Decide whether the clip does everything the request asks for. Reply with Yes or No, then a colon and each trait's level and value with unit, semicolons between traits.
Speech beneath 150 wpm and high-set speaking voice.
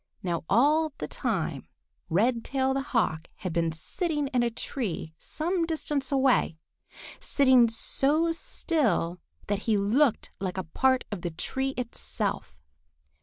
Yes: slow, 135 wpm; very high, 250 Hz